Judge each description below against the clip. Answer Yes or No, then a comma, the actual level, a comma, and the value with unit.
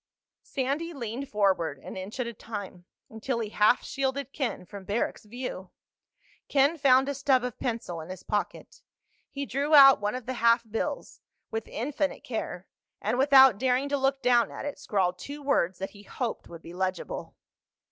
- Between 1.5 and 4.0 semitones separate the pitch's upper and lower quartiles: No, average, 5.1 semitones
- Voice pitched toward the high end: Yes, high, 240 Hz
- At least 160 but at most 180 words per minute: Yes, average, 175 wpm